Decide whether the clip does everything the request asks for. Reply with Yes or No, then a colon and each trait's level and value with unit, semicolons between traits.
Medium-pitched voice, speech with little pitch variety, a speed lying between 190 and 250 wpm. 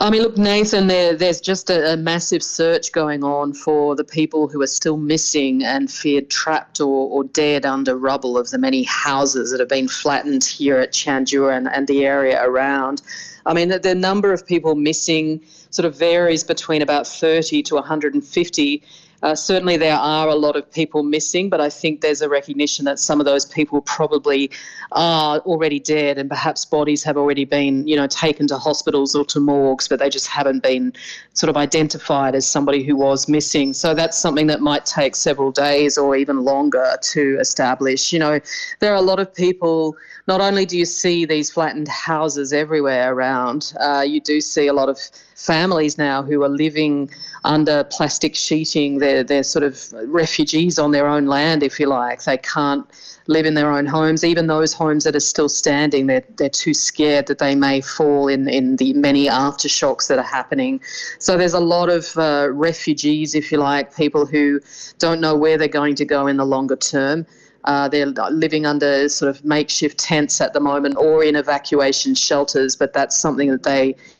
Yes: medium, 150 Hz; narrow, 2.3 semitones; average, 195 wpm